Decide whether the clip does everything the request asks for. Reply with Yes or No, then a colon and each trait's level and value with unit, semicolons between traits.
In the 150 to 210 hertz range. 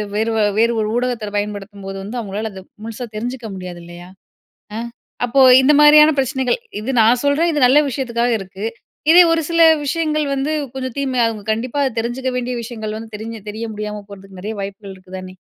No: high, 230 Hz